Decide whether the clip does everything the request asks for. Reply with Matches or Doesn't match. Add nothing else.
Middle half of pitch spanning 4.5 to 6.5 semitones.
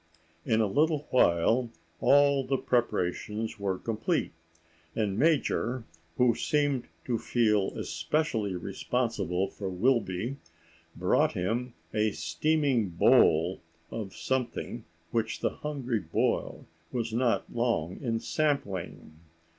Matches